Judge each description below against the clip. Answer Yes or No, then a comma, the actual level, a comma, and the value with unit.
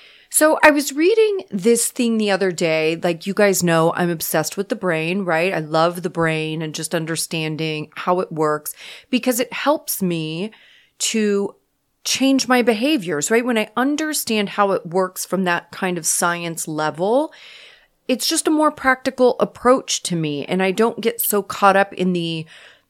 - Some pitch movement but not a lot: No, wide, 6.9 semitones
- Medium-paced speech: Yes, average, 175 wpm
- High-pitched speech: Yes, high, 195 Hz